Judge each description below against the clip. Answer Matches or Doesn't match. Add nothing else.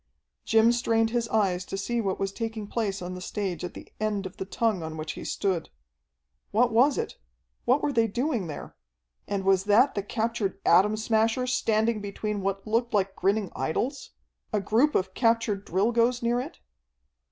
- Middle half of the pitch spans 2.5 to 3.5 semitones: Matches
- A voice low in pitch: Doesn't match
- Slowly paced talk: Doesn't match